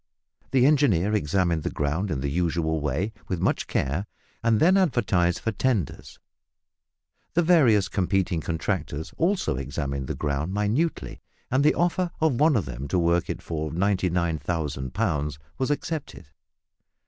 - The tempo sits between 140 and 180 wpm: Yes, average, 145 wpm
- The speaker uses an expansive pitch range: Yes, wide, 7.7 semitones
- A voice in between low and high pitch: No, very low, 90 Hz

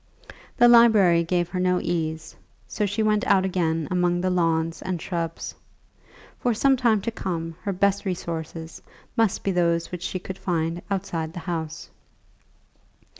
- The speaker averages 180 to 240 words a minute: No, average, 155 wpm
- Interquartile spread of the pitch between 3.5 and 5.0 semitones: No, average, 3.0 semitones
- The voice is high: No, medium, 180 Hz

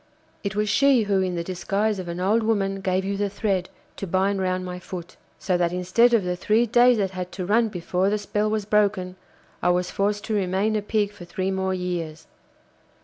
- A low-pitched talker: No, high, 195 Hz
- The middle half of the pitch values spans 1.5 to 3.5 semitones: Yes, narrow, 2.5 semitones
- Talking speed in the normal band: No, fast, 215 wpm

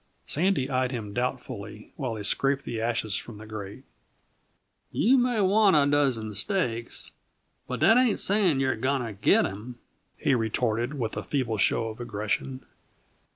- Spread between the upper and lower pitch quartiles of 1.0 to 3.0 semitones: No, average, 4.5 semitones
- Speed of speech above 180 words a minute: No, average, 155 wpm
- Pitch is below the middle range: Yes, low, 125 Hz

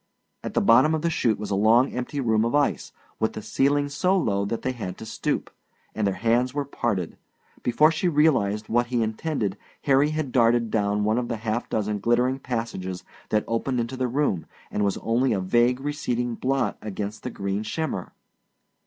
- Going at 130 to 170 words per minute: No, average, 195 wpm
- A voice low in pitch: Yes, low, 120 Hz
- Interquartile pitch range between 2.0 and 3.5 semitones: No, average, 4.0 semitones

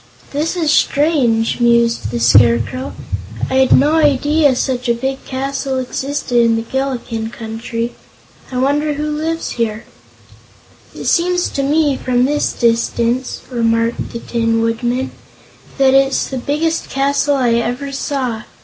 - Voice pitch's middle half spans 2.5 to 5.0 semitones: Yes, average, 3.4 semitones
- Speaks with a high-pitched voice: Yes, very high, 260 Hz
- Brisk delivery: No, slow, 135 wpm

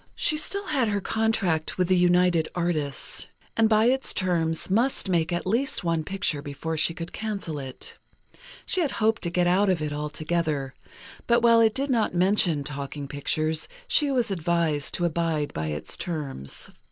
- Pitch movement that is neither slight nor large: No, wide, 6.0 semitones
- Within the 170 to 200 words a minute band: Yes, average, 175 wpm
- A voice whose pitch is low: No, medium, 175 Hz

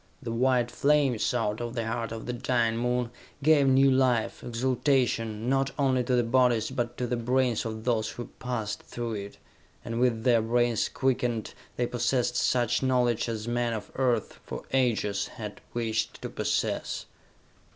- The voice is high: No, low, 120 Hz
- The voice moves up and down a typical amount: No, narrow, 1.9 semitones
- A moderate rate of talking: Yes, average, 165 wpm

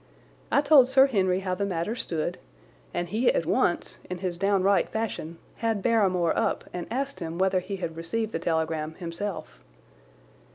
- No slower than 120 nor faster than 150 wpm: No, average, 165 wpm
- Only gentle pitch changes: No, average, 4.5 semitones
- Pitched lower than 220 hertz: Yes, medium, 185 Hz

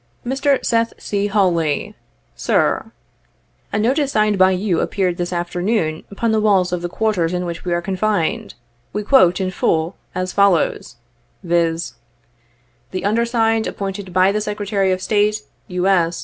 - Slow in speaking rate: No, average, 160 wpm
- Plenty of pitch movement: No, average, 3.4 semitones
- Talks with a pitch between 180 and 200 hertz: Yes, high, 190 Hz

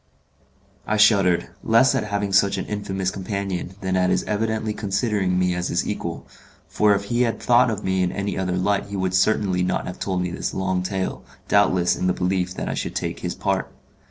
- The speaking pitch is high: No, very low, 95 Hz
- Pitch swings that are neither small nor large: No, narrow, 2.1 semitones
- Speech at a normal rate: No, fast, 210 wpm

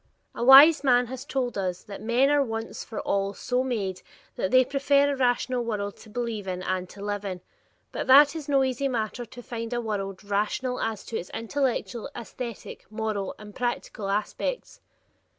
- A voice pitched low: No, high, 235 Hz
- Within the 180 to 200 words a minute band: Yes, average, 185 wpm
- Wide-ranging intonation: No, average, 4.2 semitones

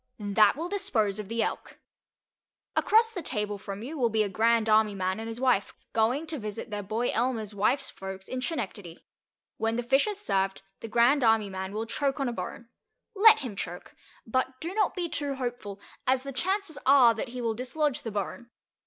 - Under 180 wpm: No, average, 200 wpm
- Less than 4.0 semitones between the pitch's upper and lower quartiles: No, average, 4.8 semitones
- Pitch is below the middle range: No, high, 235 Hz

